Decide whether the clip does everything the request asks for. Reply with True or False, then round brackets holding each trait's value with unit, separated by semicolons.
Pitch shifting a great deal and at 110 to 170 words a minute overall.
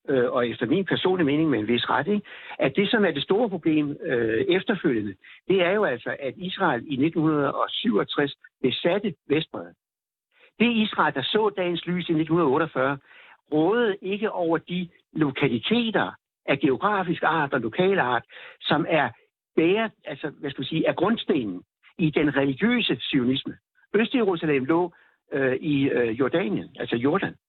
True (6.1 semitones; 150 wpm)